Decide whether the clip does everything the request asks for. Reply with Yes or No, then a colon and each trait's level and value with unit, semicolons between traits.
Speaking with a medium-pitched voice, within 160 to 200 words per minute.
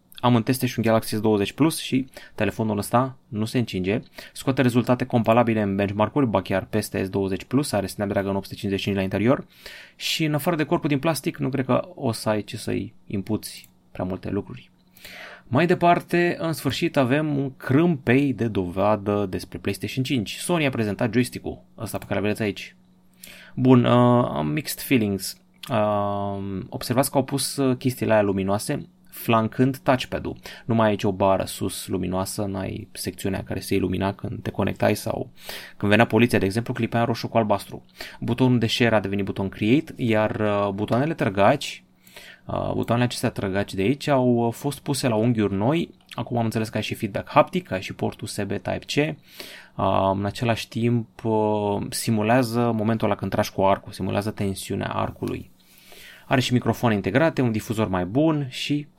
No: low, 115 Hz; fast, 170 wpm